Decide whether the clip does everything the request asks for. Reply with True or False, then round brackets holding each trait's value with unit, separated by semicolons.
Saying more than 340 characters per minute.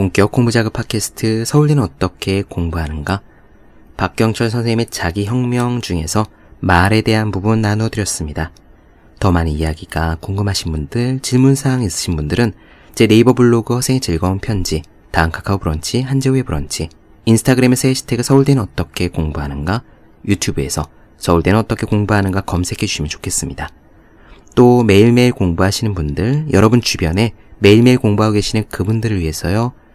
True (380 characters per minute)